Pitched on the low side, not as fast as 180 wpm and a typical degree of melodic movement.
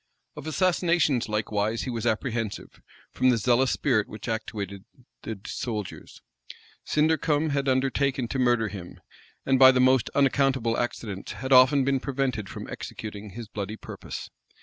Yes: low, 125 Hz; average, 145 wpm; average, 4.0 semitones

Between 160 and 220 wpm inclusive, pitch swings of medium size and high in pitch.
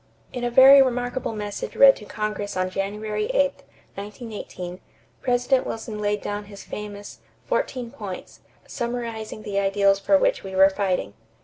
No: average, 145 wpm; average, 3.5 semitones; high, 210 Hz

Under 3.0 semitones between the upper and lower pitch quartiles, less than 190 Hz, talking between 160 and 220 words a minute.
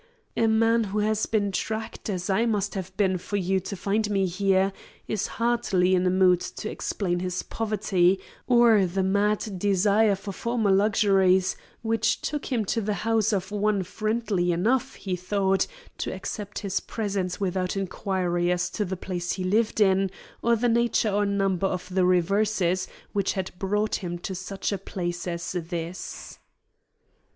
No: narrow, 2.5 semitones; high, 195 Hz; average, 165 wpm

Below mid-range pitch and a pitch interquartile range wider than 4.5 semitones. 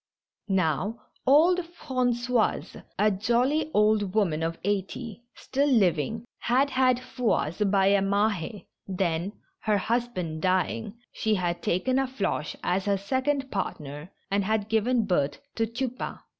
No: high, 210 Hz; average, 5.0 semitones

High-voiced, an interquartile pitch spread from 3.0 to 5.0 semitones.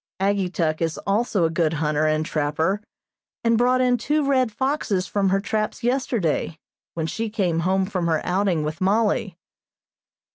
No: high, 195 Hz; wide, 5.6 semitones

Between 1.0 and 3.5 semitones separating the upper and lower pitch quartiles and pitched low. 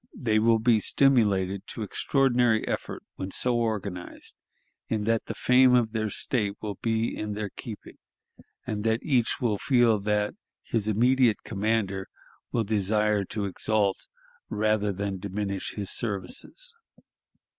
Yes: narrow, 2.4 semitones; low, 110 Hz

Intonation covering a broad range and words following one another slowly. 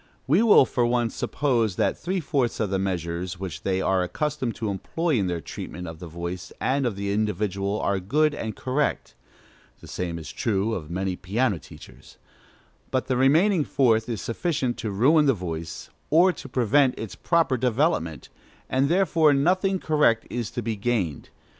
No: wide, 7.1 semitones; average, 175 wpm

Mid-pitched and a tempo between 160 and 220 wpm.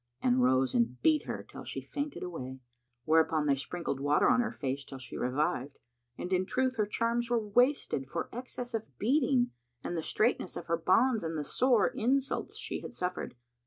Yes: medium, 180 Hz; average, 190 wpm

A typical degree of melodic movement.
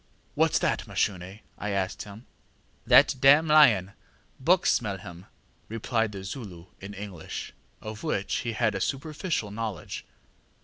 Yes: average, 4.4 semitones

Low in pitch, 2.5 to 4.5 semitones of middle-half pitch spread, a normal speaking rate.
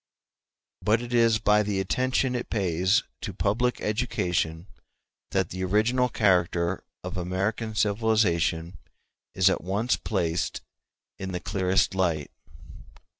No: very low, 95 Hz; average, 3.6 semitones; slow, 125 wpm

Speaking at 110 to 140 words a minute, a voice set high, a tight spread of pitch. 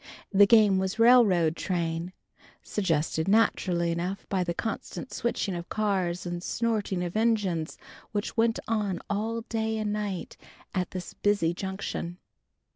No: slow, 135 wpm; high, 195 Hz; average, 3.7 semitones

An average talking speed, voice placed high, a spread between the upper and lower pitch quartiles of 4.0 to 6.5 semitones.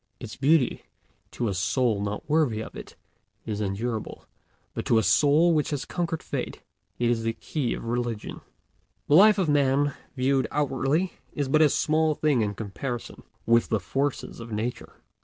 No: average, 170 wpm; low, 130 Hz; average, 4.8 semitones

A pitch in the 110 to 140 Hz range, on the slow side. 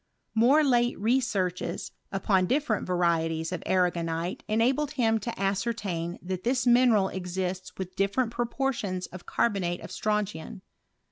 No: high, 195 Hz; slow, 125 wpm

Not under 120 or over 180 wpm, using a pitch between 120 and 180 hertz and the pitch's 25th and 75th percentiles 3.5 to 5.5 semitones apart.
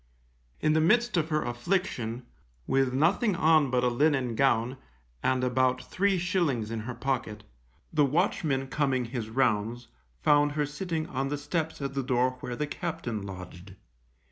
Yes: average, 160 wpm; low, 135 Hz; average, 4.4 semitones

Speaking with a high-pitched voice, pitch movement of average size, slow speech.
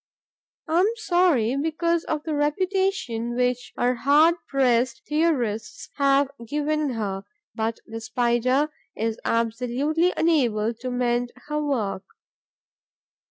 Yes: very high, 255 Hz; average, 4.7 semitones; slow, 115 wpm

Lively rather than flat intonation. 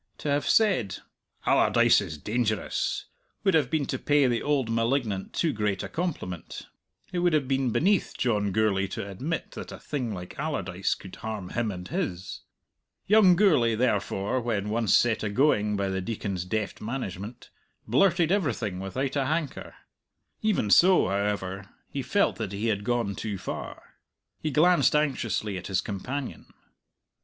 Yes: wide, 6.6 semitones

